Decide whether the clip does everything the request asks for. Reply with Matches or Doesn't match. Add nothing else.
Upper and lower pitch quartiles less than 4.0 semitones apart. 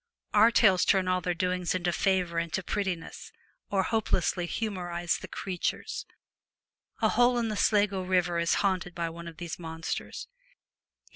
Matches